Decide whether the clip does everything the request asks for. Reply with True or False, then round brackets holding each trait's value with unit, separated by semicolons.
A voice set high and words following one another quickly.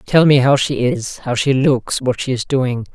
False (135 Hz; 245 wpm)